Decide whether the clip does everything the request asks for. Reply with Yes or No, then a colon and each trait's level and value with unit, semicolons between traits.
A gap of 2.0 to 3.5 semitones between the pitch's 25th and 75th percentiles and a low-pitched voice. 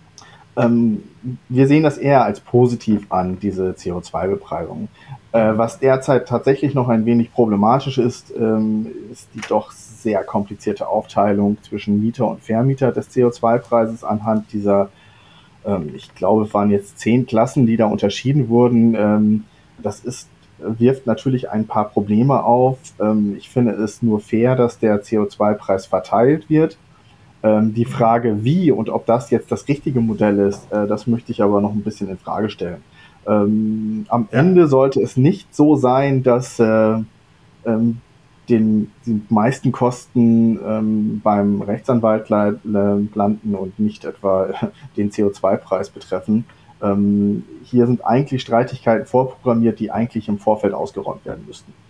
Yes: average, 2.9 semitones; low, 115 Hz